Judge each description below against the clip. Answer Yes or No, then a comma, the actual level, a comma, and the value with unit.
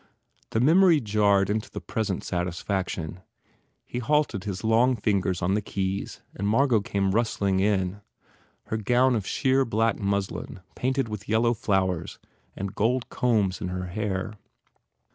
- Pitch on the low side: Yes, low, 105 Hz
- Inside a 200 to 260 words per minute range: No, average, 145 wpm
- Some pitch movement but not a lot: Yes, average, 3.5 semitones